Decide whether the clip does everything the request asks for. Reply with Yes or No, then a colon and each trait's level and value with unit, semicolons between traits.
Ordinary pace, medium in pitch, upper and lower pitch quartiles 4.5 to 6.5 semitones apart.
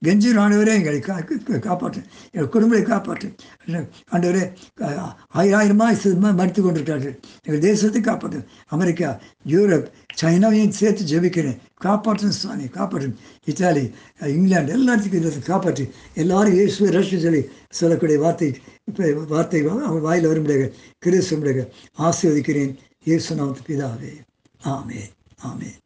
Yes: average, 100 wpm; medium, 170 Hz; average, 5.3 semitones